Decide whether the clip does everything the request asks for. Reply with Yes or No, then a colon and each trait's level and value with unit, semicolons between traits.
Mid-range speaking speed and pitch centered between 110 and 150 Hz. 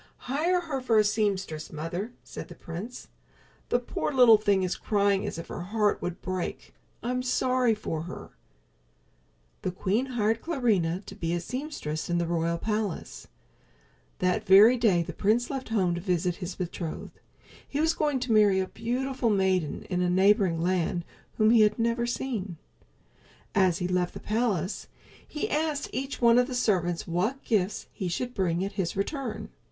No: average, 170 wpm; high, 205 Hz